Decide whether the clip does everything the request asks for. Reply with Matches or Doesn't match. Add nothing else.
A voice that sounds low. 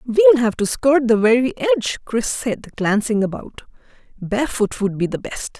Doesn't match